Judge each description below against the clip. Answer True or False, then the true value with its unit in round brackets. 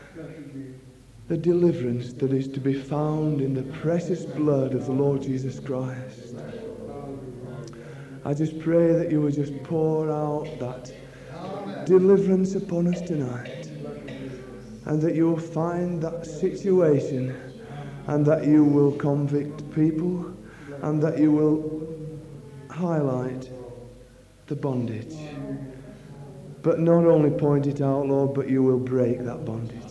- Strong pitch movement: False (3.6 semitones)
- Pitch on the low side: False (145 Hz)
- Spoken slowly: True (125 wpm)